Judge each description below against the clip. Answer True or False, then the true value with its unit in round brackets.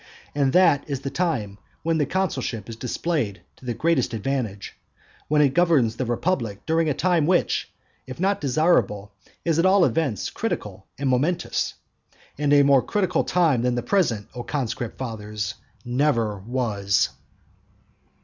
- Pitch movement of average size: False (6.2 semitones)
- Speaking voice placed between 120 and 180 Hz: True (135 Hz)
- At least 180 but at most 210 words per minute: False (150 wpm)